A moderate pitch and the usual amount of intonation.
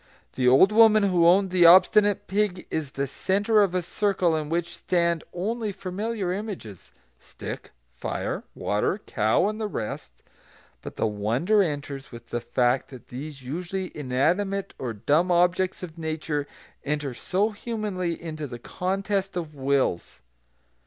No: medium, 175 Hz; wide, 6.0 semitones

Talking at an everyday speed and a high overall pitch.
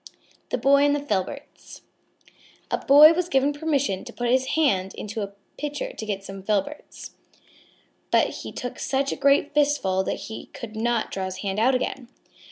Yes: average, 180 wpm; very high, 255 Hz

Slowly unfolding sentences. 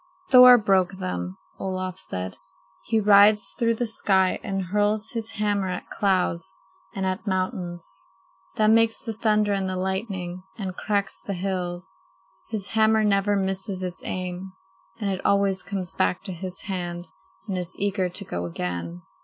No: average, 155 wpm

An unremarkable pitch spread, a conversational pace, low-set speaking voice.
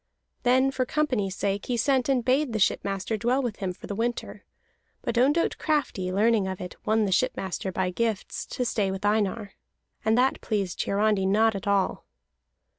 No: average, 4.2 semitones; average, 180 wpm; high, 215 Hz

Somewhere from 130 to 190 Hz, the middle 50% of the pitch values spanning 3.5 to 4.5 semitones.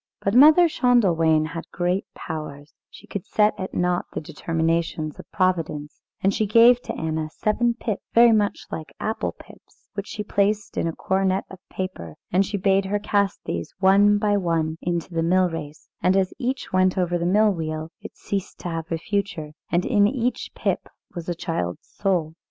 Yes: medium, 185 Hz; average, 3.9 semitones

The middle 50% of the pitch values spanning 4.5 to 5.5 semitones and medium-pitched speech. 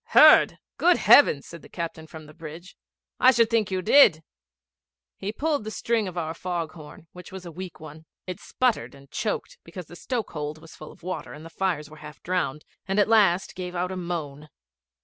No: average, 3.6 semitones; medium, 175 Hz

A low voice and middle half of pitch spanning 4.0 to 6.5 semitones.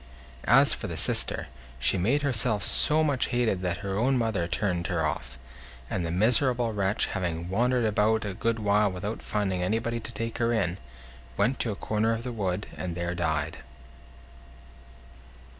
Yes: low, 105 Hz; average, 4.4 semitones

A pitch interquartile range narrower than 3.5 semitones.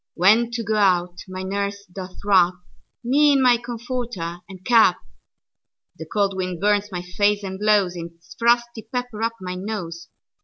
No: average, 4.1 semitones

